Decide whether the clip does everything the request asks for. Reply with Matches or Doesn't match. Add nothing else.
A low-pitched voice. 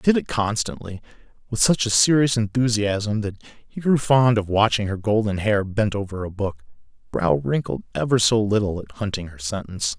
Matches